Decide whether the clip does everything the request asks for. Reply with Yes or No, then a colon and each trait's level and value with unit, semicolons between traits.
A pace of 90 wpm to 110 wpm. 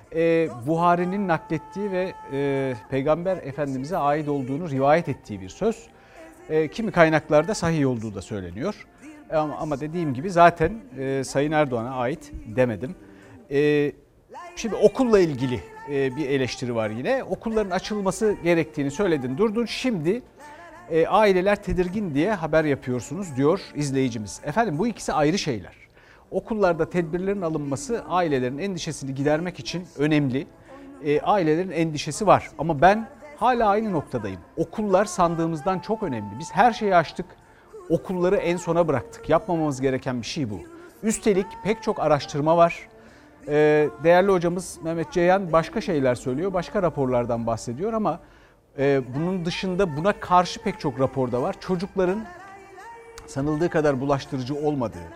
No: average, 125 wpm